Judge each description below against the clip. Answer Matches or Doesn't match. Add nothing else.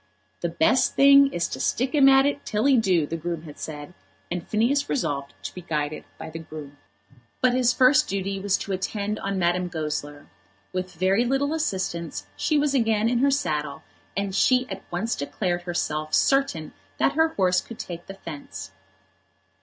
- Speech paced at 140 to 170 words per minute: Doesn't match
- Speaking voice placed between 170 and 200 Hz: Matches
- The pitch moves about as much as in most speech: Doesn't match